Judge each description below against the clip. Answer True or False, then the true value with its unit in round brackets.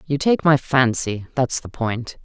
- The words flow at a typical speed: True (190 wpm)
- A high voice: False (130 Hz)